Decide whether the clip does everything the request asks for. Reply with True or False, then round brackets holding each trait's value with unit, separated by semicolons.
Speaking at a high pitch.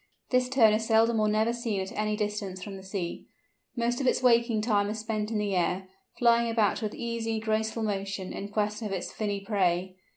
True (215 Hz)